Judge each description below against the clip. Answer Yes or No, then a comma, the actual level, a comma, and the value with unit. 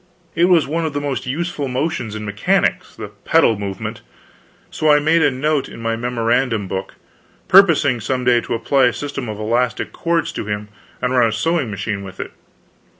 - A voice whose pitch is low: Yes, low, 125 Hz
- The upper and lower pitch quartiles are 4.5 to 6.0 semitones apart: Yes, average, 5.1 semitones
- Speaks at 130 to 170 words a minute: No, average, 190 wpm